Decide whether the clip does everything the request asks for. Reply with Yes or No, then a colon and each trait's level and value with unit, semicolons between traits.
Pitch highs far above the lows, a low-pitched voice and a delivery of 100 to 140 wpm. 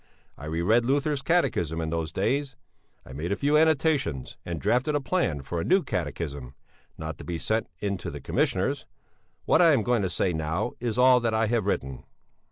No: wide, 8.8 semitones; low, 105 Hz; average, 195 wpm